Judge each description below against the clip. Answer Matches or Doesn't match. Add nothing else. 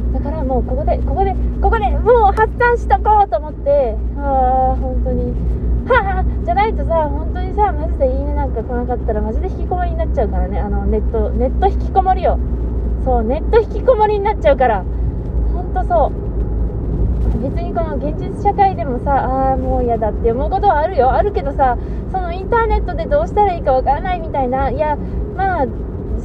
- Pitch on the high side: Matches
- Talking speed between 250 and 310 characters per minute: Doesn't match